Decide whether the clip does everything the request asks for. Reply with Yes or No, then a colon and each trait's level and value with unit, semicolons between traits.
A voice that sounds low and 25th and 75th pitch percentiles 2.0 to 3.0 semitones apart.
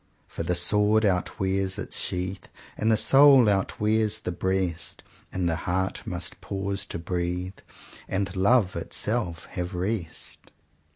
Yes: very low, 95 Hz; average, 2.7 semitones